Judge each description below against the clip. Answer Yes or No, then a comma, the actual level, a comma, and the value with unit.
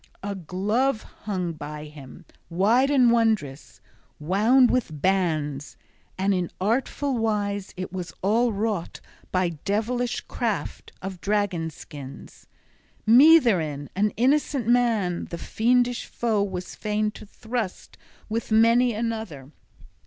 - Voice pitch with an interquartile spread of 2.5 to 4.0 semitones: No, average, 4.8 semitones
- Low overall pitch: No, high, 210 Hz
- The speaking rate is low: Yes, slow, 125 wpm